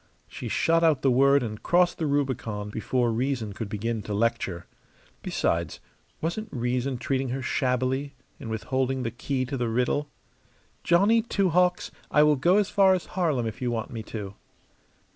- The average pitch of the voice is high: No, low, 130 Hz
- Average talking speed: Yes, average, 170 wpm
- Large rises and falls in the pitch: No, average, 4.7 semitones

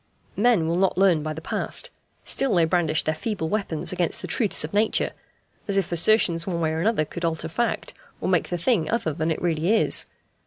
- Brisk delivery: Yes, fast, 210 wpm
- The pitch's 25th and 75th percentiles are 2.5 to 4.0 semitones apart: No, average, 4.4 semitones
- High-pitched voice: No, medium, 170 Hz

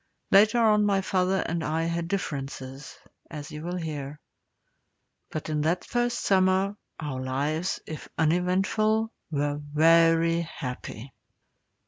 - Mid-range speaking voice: Yes, medium, 165 Hz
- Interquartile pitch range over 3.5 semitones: Yes, average, 4.3 semitones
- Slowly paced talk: Yes, slow, 120 wpm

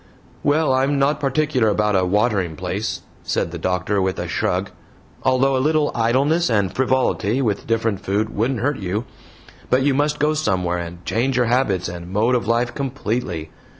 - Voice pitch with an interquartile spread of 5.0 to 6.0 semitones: Yes, wide, 5.6 semitones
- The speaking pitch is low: Yes, low, 115 Hz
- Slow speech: No, average, 175 wpm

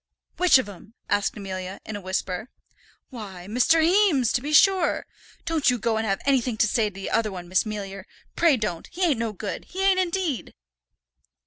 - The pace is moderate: Yes, average, 195 wpm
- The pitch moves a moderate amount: No, wide, 8.1 semitones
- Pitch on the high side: Yes, high, 225 Hz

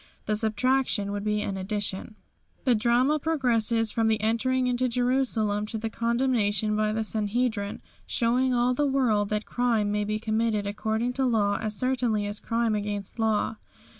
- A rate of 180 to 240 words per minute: No, average, 165 wpm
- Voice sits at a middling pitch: No, high, 220 Hz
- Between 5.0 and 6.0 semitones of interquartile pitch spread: No, average, 2.8 semitones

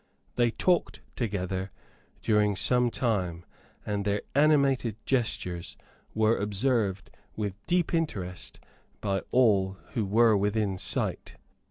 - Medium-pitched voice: No, low, 105 Hz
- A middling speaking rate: No, slow, 110 wpm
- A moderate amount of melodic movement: Yes, average, 4.0 semitones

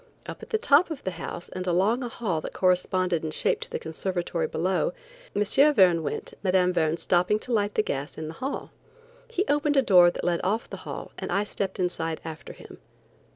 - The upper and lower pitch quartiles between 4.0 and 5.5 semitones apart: Yes, average, 4.4 semitones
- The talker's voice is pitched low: No, medium, 185 Hz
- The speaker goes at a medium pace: No, fast, 210 wpm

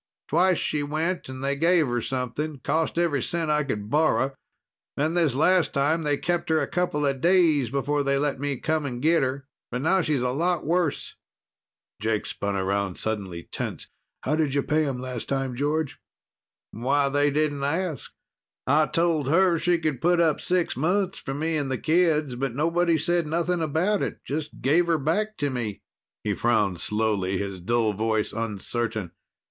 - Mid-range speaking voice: Yes, medium, 145 Hz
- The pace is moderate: Yes, average, 175 wpm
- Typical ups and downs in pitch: Yes, average, 4.6 semitones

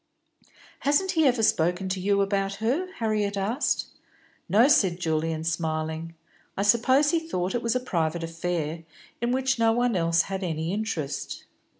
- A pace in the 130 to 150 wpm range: No, average, 160 wpm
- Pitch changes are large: Yes, wide, 6.2 semitones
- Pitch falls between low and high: No, high, 195 Hz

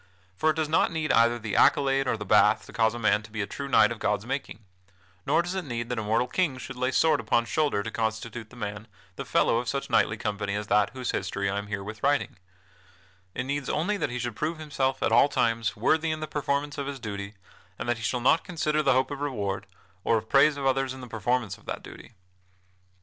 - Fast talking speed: Yes, fast, 240 wpm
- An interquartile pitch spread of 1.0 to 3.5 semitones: No, average, 4.6 semitones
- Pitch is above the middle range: No, low, 120 Hz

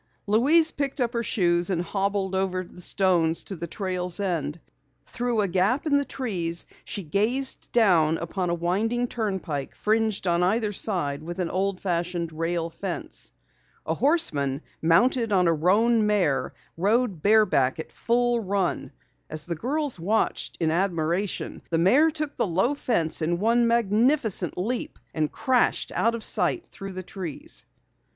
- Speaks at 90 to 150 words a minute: No, average, 160 wpm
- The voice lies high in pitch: Yes, high, 195 Hz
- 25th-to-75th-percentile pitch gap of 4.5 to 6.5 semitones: Yes, average, 5.3 semitones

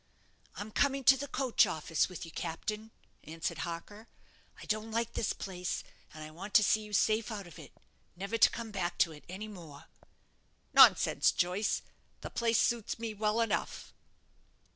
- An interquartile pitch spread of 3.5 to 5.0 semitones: Yes, average, 4.4 semitones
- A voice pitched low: No, high, 210 Hz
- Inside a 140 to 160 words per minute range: No, average, 170 wpm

